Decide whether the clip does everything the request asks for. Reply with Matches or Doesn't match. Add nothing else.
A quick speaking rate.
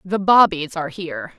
Doesn't match